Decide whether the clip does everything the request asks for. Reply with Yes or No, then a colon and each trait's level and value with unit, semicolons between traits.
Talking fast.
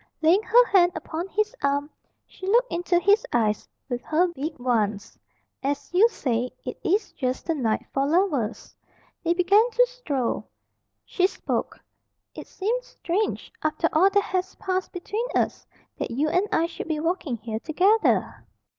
No: average, 160 wpm